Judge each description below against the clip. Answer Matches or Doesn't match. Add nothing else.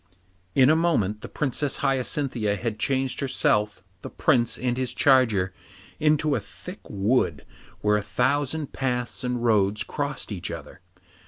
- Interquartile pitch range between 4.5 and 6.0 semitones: Matches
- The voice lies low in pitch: Matches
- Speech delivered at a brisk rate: Doesn't match